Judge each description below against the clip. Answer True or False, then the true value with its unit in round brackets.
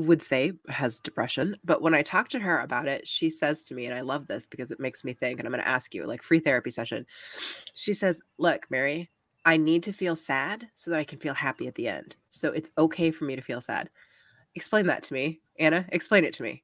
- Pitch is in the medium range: True (160 Hz)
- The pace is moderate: False (255 wpm)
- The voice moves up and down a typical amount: True (3.1 semitones)